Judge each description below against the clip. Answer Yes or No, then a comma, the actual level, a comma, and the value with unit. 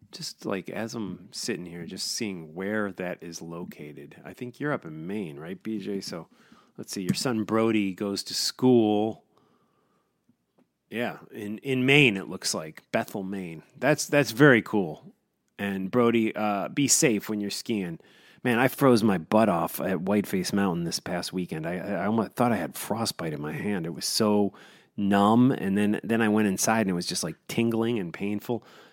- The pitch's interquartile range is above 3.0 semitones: Yes, average, 3.5 semitones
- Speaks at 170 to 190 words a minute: Yes, average, 185 wpm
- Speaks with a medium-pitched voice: No, low, 105 Hz